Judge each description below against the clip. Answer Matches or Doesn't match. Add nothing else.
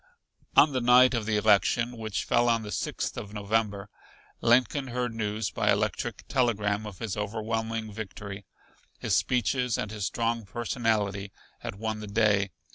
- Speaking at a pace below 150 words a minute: Doesn't match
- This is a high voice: Doesn't match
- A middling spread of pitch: Doesn't match